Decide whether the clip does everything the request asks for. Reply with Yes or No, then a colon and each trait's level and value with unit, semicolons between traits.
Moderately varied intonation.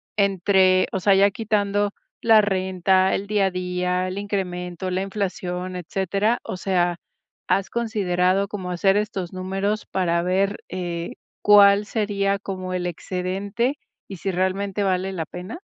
No: narrow, 1.8 semitones